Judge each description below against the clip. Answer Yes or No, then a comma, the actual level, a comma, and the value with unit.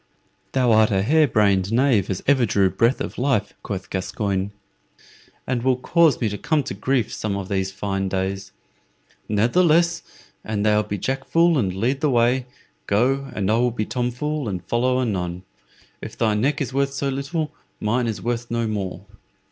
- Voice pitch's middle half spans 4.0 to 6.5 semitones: Yes, average, 5.1 semitones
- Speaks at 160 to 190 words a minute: Yes, average, 180 wpm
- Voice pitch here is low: Yes, low, 115 Hz